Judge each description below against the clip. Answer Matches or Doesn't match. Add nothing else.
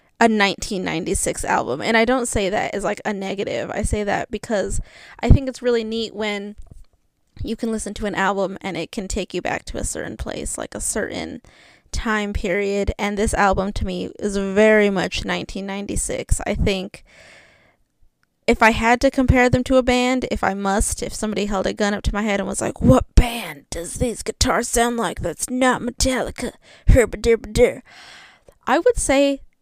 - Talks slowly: Doesn't match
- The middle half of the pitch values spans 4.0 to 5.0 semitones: Doesn't match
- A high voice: Matches